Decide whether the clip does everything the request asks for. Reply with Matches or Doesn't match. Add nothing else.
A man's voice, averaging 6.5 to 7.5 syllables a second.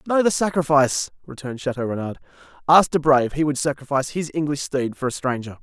Matches